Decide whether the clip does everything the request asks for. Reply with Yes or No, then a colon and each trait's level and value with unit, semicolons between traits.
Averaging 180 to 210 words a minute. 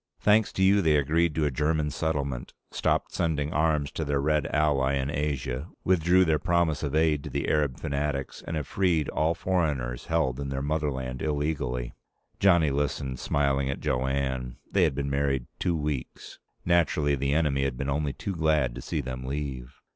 Yes: average, 185 wpm